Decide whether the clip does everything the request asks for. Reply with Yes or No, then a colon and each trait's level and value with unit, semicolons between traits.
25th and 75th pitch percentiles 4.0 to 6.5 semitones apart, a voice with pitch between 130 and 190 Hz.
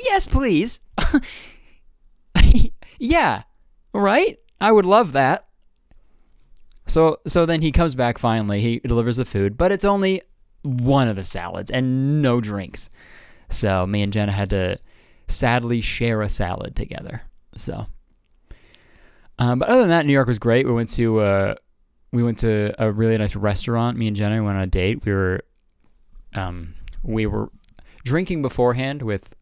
No: average, 5.3 semitones; low, 115 Hz